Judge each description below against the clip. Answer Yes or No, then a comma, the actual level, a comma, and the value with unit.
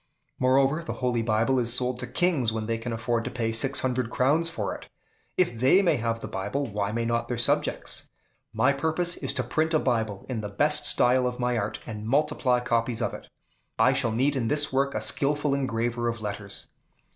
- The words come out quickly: Yes, fast, 210 wpm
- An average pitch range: Yes, average, 3.3 semitones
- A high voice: No, low, 125 Hz